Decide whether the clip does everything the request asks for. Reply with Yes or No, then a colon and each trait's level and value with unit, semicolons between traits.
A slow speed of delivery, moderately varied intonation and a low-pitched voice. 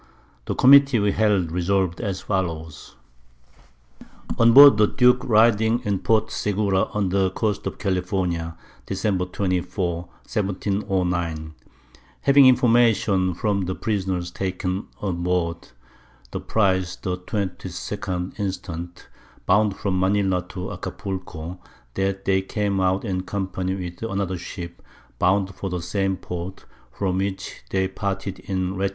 No: slow, 125 wpm; narrow, 2.1 semitones; very low, 95 Hz